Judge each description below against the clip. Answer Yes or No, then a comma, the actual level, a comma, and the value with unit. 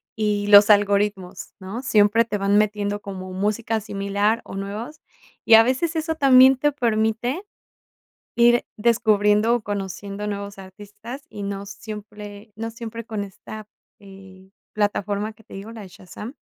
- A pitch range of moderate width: No, narrow, 2.2 semitones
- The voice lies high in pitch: Yes, high, 210 Hz